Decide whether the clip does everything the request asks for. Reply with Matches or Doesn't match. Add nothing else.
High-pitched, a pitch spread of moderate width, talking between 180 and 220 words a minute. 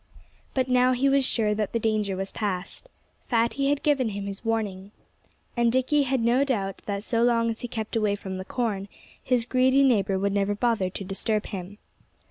Matches